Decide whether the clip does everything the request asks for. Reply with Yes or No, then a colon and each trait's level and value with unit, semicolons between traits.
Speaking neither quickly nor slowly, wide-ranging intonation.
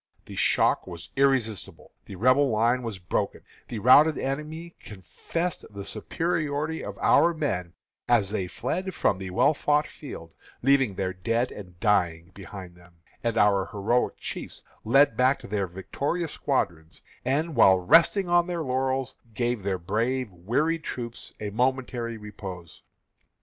Yes: average, 145 wpm; wide, 6.7 semitones